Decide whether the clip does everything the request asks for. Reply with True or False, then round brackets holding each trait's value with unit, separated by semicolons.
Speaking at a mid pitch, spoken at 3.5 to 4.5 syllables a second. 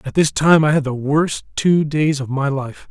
True (145 Hz; 4.4 syllables/s)